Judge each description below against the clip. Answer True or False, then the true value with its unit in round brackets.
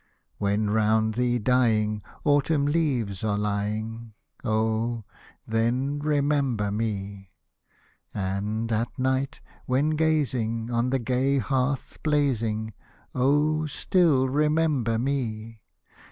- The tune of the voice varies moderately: True (4.4 semitones)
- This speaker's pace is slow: True (95 wpm)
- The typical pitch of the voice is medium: False (120 Hz)